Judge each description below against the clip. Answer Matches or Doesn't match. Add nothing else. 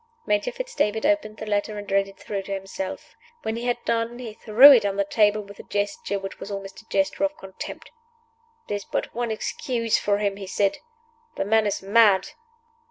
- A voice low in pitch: Doesn't match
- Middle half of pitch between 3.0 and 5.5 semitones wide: Doesn't match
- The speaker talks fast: Matches